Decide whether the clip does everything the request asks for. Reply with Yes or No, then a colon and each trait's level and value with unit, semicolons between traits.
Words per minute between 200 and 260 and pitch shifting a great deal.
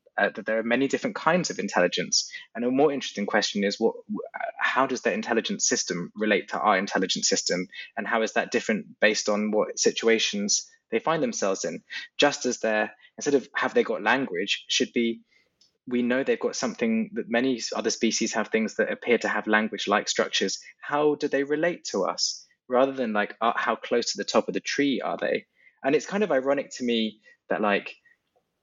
Yes: fast, 205 wpm; wide, 7.7 semitones